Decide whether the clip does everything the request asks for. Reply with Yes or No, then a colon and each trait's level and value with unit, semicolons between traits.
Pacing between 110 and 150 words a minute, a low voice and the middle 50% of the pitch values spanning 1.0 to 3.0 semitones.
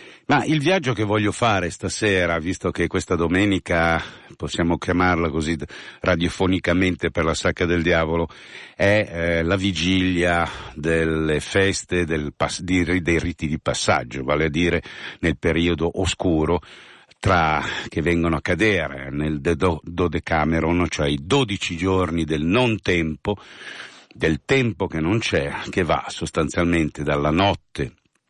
Yes: average, 140 wpm; very low, 85 Hz; narrow, 2.5 semitones